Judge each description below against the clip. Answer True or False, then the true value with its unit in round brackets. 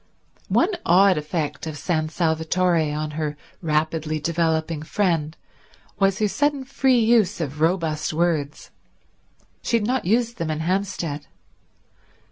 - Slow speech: True (125 wpm)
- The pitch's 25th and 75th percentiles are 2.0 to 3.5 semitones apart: False (4.1 semitones)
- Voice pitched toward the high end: False (165 Hz)